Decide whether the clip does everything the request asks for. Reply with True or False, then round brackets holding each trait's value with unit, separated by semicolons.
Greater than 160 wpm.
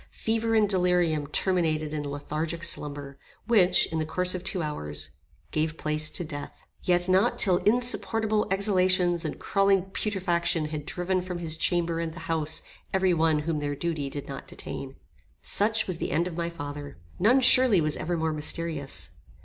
True (170 wpm)